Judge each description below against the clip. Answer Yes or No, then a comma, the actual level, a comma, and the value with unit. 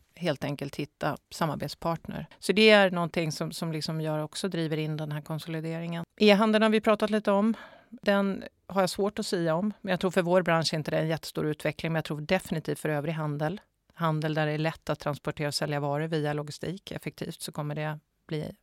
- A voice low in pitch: No, medium, 165 Hz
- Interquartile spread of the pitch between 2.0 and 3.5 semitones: No, average, 4.1 semitones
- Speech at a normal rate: No, fast, 220 wpm